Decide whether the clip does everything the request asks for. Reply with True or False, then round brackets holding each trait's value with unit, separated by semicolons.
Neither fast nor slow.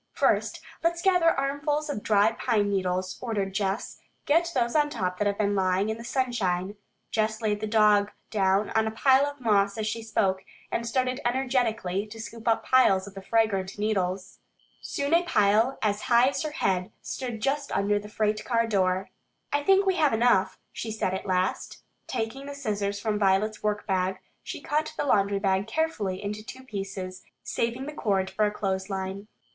True (185 wpm)